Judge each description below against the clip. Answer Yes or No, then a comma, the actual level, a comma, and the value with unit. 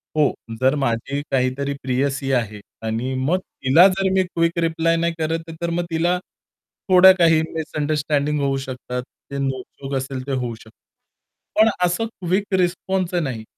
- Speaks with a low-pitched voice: No, medium, 150 Hz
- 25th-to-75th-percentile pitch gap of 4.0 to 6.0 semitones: Yes, average, 4.6 semitones